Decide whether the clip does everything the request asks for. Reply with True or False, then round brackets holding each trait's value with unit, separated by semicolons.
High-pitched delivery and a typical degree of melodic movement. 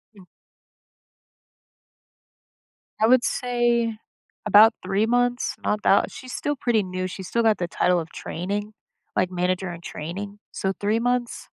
True (205 Hz; 4.3 semitones)